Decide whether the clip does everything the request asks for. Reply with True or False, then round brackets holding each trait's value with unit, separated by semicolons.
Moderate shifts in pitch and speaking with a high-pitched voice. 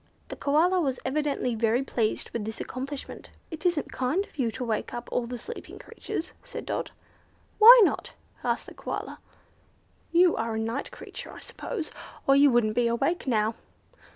False (5.8 semitones; 265 Hz)